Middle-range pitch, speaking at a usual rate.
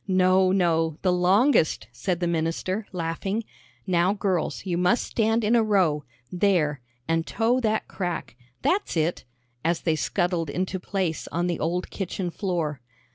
Yes: medium, 180 Hz; average, 150 wpm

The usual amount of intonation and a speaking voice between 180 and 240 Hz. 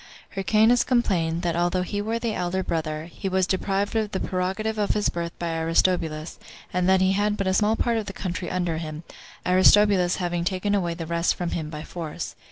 Yes: average, 3.3 semitones; medium, 185 Hz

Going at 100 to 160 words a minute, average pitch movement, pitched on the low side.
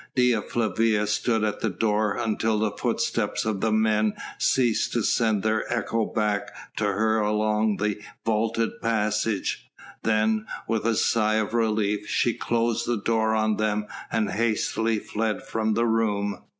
No: average, 150 wpm; narrow, 1.2 semitones; low, 110 Hz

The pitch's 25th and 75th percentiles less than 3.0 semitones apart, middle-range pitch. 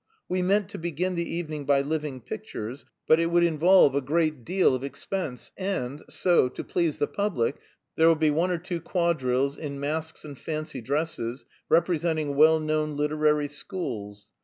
No: average, 3.4 semitones; medium, 155 Hz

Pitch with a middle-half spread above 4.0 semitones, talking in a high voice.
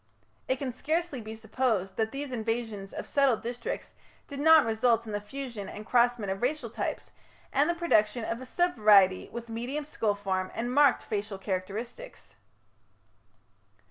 Yes: average, 4.4 semitones; high, 235 Hz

